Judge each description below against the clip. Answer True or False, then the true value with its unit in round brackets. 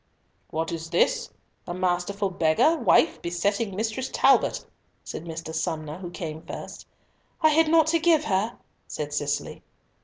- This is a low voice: False (185 Hz)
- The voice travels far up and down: True (7.8 semitones)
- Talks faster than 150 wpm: False (145 wpm)